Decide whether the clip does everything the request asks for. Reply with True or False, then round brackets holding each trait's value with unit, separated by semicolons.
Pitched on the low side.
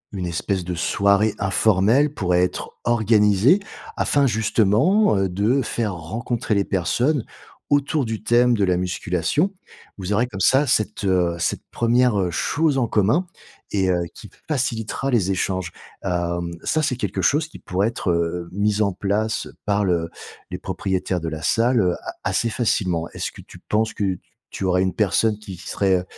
True (100 Hz)